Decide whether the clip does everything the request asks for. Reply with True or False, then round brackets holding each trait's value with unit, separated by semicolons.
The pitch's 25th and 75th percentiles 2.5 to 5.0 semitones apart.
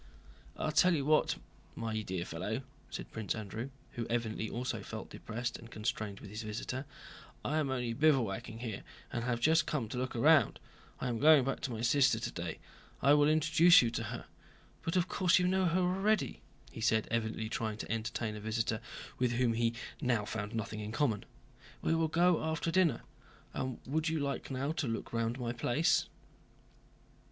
False (5.4 semitones)